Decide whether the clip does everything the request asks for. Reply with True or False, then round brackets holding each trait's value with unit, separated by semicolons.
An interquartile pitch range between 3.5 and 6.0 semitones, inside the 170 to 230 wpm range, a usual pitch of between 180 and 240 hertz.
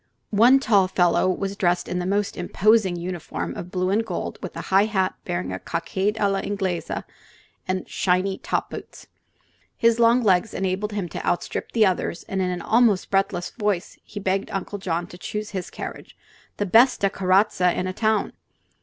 False (2.6 semitones; 180 wpm; 190 Hz)